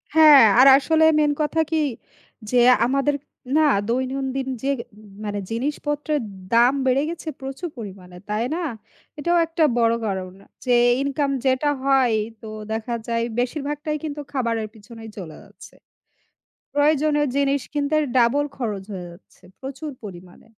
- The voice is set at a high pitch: Yes, very high, 270 Hz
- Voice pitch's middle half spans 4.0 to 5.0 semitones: Yes, average, 4.3 semitones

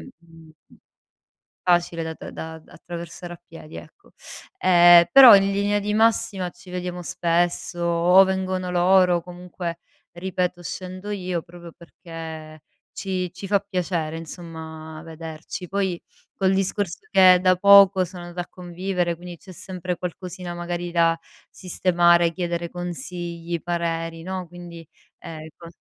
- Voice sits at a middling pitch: Yes, medium, 175 Hz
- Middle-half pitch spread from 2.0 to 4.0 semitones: No, narrow, 1.6 semitones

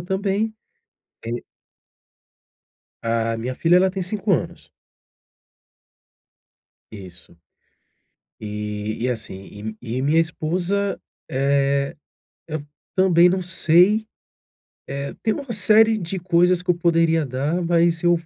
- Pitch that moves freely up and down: Yes, wide, 6.3 semitones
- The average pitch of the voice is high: No, medium, 165 Hz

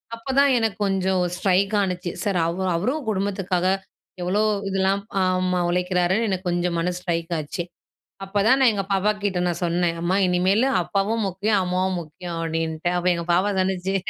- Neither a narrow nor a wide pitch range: No, narrow, 2.1 semitones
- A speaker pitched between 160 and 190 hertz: Yes, medium, 185 Hz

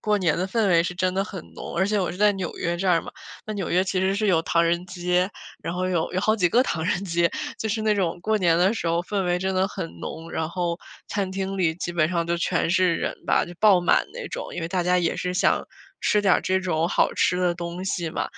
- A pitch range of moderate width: No, narrow, 2.0 semitones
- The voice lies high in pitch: No, medium, 180 Hz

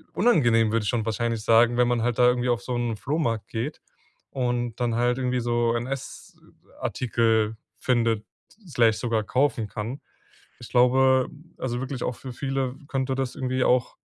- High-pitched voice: No, low, 120 Hz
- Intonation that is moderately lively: No, narrow, 2.0 semitones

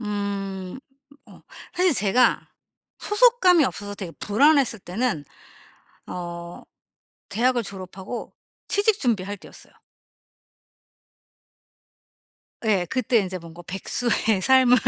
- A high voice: Yes, high, 210 Hz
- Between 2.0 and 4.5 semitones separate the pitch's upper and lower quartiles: No, average, 5.2 semitones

